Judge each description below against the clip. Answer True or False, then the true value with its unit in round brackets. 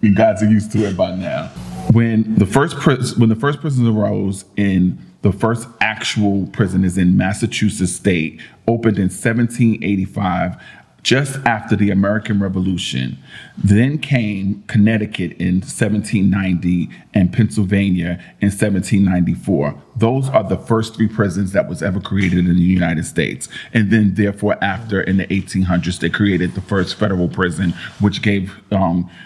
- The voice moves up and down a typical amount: True (3.1 semitones)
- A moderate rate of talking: True (150 wpm)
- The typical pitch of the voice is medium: False (100 Hz)